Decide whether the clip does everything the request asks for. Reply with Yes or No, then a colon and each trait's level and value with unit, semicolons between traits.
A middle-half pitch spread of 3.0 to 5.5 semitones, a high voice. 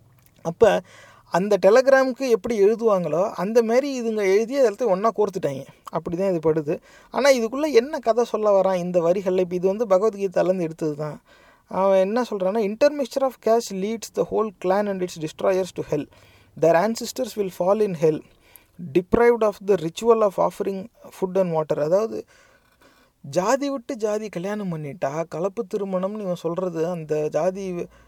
Yes: average, 4.9 semitones; high, 195 Hz